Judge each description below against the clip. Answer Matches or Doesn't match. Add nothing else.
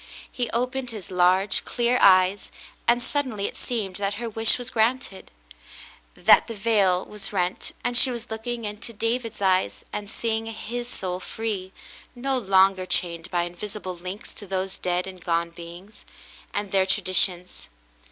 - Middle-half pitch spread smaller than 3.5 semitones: Doesn't match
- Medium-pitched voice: Doesn't match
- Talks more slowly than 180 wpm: Matches